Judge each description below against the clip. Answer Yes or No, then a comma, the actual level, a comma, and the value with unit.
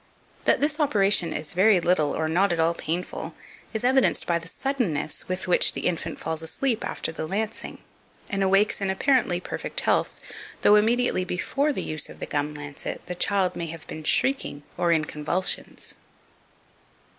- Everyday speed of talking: Yes, average, 170 wpm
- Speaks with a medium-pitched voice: Yes, medium, 180 Hz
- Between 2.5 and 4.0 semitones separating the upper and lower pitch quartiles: No, average, 4.6 semitones